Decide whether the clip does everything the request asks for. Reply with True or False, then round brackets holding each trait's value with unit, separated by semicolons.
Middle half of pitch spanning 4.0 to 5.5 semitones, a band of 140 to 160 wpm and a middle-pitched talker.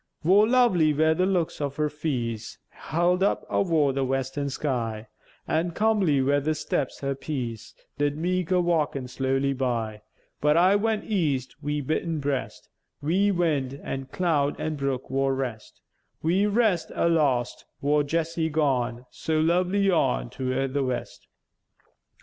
True (4.4 semitones; 145 wpm; 150 Hz)